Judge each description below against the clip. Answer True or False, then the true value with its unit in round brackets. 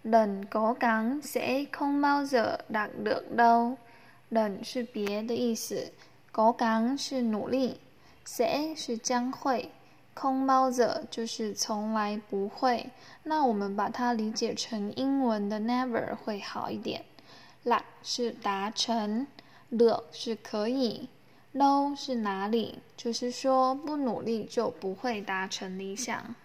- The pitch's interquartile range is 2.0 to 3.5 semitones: True (2.9 semitones)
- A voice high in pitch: True (235 Hz)